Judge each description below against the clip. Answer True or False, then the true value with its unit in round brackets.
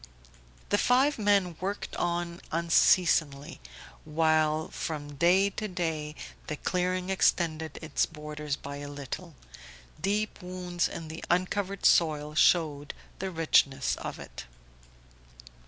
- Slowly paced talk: True (115 wpm)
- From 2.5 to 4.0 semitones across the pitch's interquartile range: True (3.3 semitones)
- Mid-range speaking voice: True (170 Hz)